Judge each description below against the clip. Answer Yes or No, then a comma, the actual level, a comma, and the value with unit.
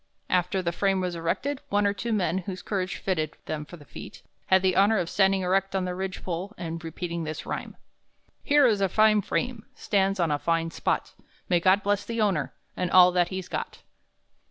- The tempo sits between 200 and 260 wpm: Yes, fast, 205 wpm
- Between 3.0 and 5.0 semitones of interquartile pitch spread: No, narrow, 2.6 semitones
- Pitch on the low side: No, medium, 185 Hz